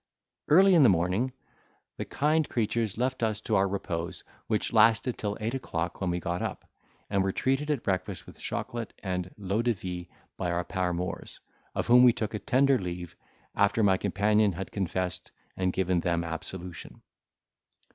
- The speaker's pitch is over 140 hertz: No, low, 100 Hz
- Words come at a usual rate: Yes, average, 170 wpm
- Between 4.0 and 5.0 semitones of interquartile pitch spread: Yes, average, 4.3 semitones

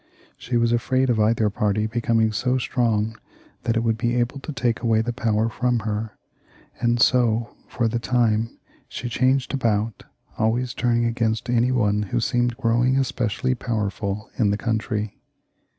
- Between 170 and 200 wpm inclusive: No, average, 160 wpm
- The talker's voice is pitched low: Yes, low, 115 Hz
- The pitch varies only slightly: Yes, narrow, 1.9 semitones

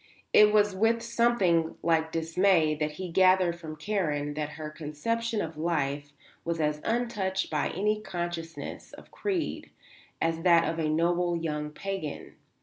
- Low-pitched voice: No, medium, 170 Hz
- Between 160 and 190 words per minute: No, average, 145 wpm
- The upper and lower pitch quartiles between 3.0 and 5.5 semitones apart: Yes, average, 4.1 semitones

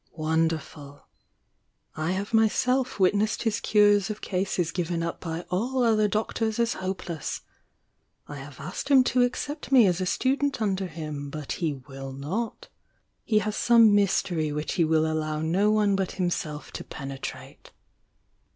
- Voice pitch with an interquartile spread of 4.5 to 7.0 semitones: Yes, wide, 5.4 semitones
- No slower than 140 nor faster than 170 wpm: Yes, average, 155 wpm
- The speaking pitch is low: No, medium, 185 Hz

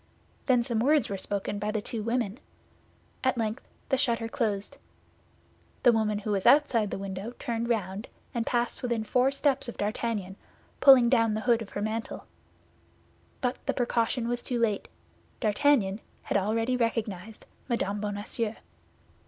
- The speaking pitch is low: No, high, 225 Hz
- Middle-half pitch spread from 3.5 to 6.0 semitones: No, narrow, 2.6 semitones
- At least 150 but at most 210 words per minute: Yes, average, 155 wpm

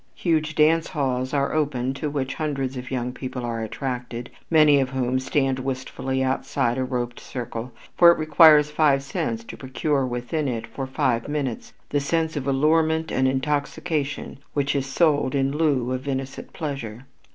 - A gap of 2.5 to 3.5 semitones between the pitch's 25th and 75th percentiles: Yes, average, 2.8 semitones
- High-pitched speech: No, low, 135 Hz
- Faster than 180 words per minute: No, average, 165 wpm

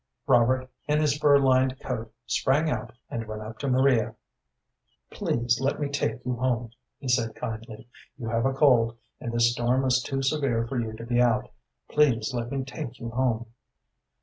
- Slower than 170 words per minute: No, average, 180 wpm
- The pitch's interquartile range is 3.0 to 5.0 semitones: No, narrow, 2.5 semitones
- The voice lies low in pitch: Yes, low, 125 Hz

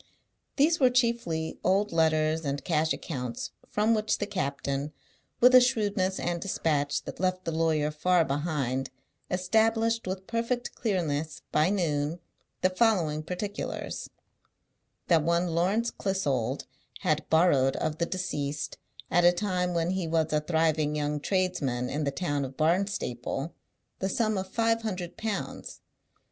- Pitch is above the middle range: No, medium, 170 Hz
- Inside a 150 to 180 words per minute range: No, average, 140 wpm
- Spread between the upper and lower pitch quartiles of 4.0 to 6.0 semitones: Yes, average, 4.6 semitones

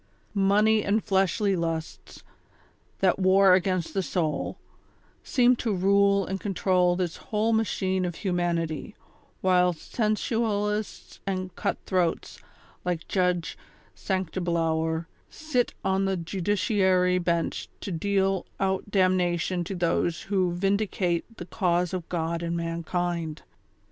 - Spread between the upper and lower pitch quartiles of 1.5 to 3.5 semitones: Yes, narrow, 2.5 semitones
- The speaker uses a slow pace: Yes, slow, 120 wpm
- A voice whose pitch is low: No, medium, 185 Hz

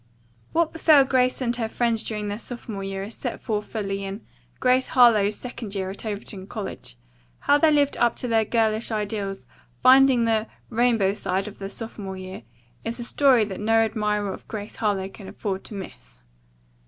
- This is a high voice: Yes, high, 220 Hz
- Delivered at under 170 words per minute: No, average, 180 wpm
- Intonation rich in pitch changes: No, average, 3.3 semitones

